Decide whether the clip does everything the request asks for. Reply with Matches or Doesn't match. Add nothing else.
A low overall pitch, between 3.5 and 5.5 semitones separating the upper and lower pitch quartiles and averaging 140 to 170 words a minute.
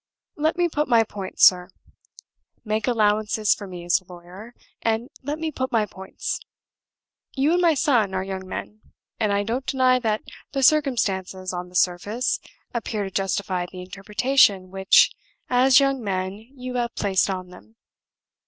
Doesn't match